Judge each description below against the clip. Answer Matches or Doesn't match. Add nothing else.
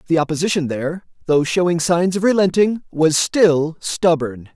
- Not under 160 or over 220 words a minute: Doesn't match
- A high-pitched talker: Doesn't match